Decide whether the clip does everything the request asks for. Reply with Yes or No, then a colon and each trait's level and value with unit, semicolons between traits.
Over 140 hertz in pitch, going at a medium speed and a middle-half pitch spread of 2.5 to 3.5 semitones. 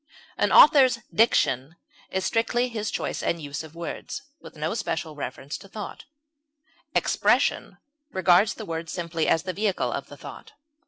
No: medium, 185 Hz; average, 155 wpm; average, 5.2 semitones